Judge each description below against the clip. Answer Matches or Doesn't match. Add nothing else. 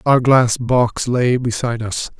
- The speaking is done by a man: Matches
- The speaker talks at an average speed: Matches